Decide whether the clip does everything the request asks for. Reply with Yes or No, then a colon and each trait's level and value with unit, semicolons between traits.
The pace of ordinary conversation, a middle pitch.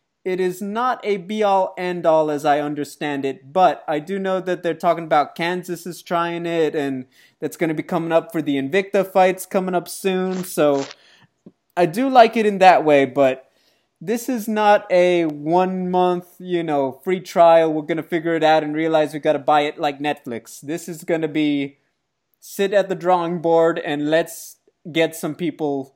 Yes: average, 190 wpm; medium, 170 Hz